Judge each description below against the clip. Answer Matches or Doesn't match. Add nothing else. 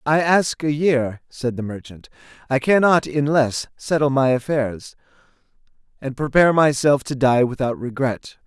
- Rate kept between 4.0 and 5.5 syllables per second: Matches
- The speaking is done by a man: Matches